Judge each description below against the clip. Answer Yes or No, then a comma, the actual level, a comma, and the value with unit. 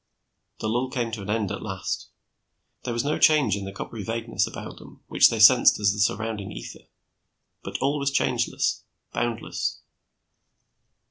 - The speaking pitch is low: Yes, low, 115 Hz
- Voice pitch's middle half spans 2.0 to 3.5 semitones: Yes, average, 2.9 semitones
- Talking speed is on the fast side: No, average, 160 wpm